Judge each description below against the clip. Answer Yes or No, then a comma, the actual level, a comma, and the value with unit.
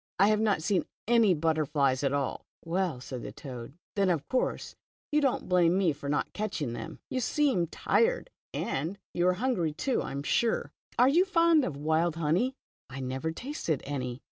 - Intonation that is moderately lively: No, wide, 8.2 semitones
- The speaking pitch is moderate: Yes, medium, 170 Hz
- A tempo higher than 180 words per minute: Yes, average, 190 wpm